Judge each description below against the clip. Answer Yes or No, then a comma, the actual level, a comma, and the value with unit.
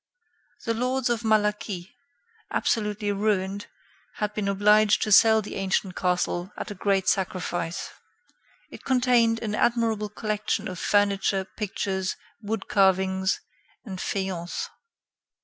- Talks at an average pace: No, slow, 115 wpm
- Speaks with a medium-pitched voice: No, high, 205 Hz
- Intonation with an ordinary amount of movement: No, narrow, 2.3 semitones